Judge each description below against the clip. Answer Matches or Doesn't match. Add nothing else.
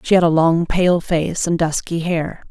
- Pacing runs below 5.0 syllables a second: Matches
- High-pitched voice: Doesn't match